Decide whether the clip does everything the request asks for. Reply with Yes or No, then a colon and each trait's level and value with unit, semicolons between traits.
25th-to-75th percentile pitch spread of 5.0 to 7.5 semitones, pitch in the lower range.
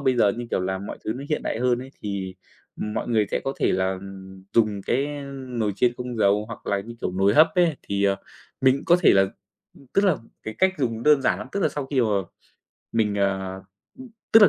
Yes: average, 5.3 semitones; low, 115 Hz